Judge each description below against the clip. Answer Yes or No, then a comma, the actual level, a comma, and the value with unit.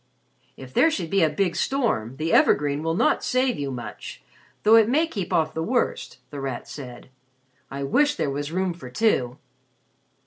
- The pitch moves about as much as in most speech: No, wide, 7.9 semitones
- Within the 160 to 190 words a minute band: Yes, average, 180 wpm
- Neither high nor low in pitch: Yes, medium, 160 Hz